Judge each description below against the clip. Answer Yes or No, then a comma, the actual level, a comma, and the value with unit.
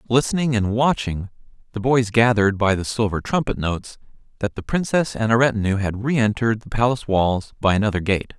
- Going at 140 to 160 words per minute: No, average, 180 wpm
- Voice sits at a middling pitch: No, low, 110 Hz